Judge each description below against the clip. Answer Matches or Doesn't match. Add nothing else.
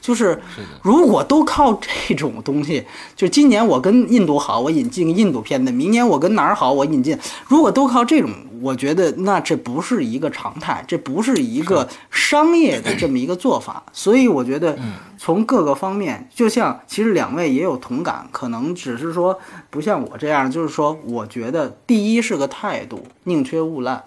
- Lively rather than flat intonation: Matches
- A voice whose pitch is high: Matches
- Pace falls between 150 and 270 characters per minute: Doesn't match